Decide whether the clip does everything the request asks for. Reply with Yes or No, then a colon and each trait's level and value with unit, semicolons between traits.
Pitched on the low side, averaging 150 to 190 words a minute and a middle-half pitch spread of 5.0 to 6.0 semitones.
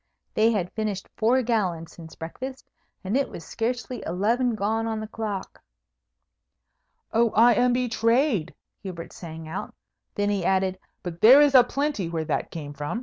No: high, 215 Hz; average, 160 wpm; average, 5.3 semitones